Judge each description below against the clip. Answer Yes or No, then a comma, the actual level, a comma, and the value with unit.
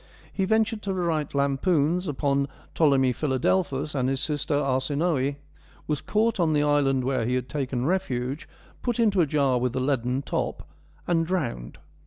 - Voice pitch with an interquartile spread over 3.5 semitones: Yes, average, 4.5 semitones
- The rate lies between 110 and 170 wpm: Yes, average, 160 wpm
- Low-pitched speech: No, medium, 145 Hz